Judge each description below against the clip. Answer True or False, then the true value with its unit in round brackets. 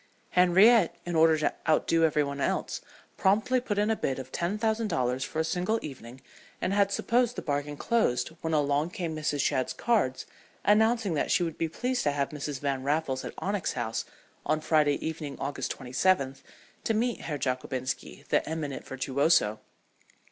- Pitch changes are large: True (6.2 semitones)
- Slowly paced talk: False (175 wpm)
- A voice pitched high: False (155 Hz)